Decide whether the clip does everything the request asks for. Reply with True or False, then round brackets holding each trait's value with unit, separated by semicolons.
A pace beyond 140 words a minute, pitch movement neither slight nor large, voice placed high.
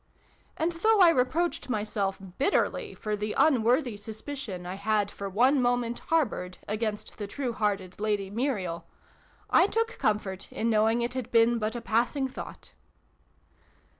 True (155 wpm; 4.1 semitones; 225 Hz)